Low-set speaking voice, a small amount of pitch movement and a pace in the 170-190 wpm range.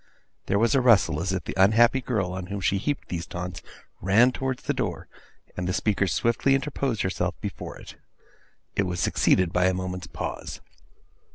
No: very low, 95 Hz; average, 4.6 semitones; average, 180 wpm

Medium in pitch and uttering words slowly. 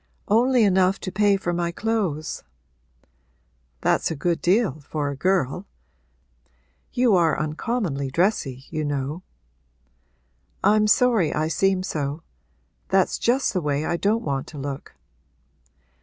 Yes: medium, 175 Hz; slow, 125 wpm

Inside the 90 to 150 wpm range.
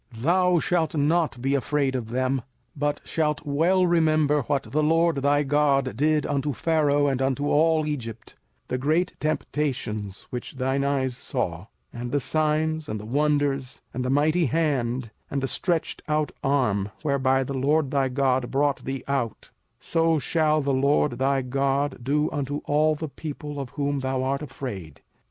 No: average, 170 wpm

